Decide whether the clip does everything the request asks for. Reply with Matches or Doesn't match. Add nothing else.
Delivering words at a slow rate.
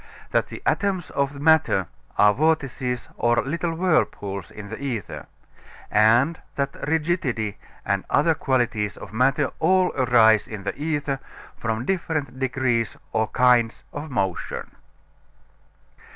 Matches